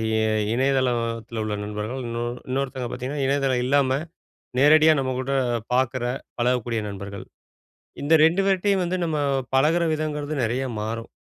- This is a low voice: Yes, low, 130 Hz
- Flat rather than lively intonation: No, average, 3.8 semitones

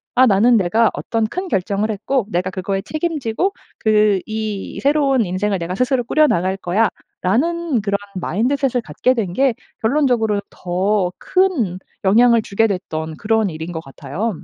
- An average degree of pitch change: Yes, average, 4.9 semitones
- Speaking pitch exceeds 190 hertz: Yes, high, 215 Hz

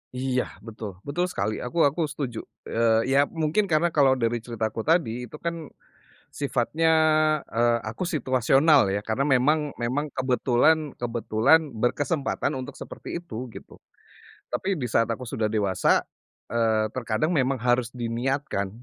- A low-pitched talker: Yes, low, 130 Hz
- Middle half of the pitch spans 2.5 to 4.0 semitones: No, average, 4.6 semitones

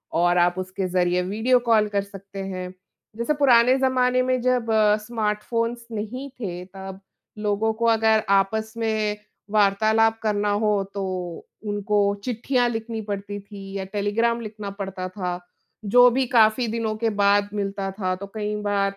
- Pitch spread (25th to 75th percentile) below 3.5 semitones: Yes, average, 2.7 semitones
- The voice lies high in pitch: Yes, high, 210 Hz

